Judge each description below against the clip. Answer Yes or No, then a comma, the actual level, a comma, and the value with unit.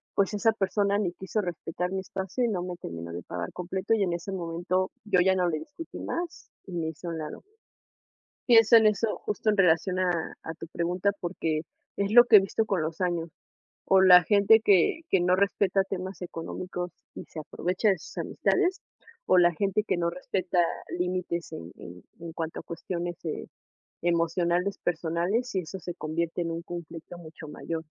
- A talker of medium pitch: Yes, medium, 180 Hz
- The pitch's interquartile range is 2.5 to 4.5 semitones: Yes, average, 2.8 semitones